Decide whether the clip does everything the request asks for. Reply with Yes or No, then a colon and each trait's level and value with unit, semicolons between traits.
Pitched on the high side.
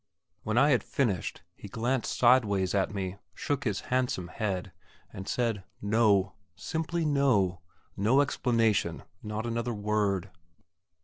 No: low, 110 Hz